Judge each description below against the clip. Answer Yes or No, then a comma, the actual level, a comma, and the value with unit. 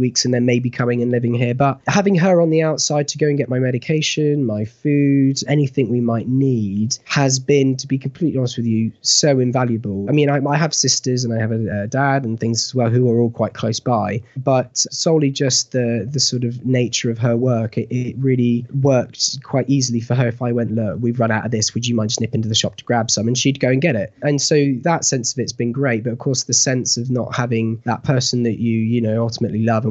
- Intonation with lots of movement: No, average, 2.9 semitones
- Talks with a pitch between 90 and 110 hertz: No, low, 125 Hz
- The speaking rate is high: Yes, fast, 255 wpm